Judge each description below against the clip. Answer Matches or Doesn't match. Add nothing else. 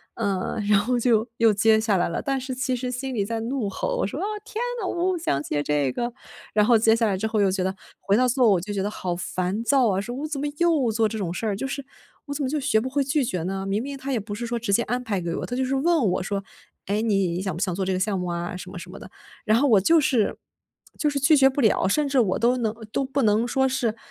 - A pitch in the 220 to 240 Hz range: Matches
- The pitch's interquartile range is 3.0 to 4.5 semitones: Doesn't match